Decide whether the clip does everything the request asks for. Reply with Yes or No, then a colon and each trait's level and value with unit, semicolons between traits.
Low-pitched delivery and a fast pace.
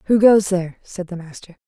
No: high, 190 Hz; fast, 215 wpm